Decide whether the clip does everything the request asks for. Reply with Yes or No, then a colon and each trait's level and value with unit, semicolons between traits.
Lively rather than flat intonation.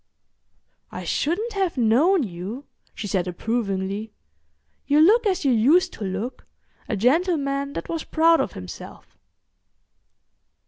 Yes: wide, 7.9 semitones